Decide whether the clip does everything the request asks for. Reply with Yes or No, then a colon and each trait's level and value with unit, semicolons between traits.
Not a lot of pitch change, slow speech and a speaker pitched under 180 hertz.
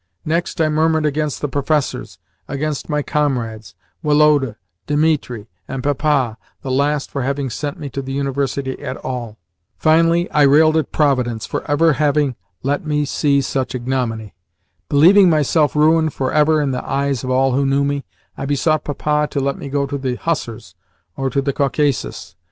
No: narrow, 2.2 semitones; average, 170 wpm; medium, 140 Hz